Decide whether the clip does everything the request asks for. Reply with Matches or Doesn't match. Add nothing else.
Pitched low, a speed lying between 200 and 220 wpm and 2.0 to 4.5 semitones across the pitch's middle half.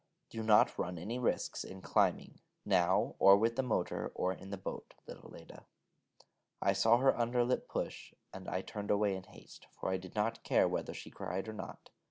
Matches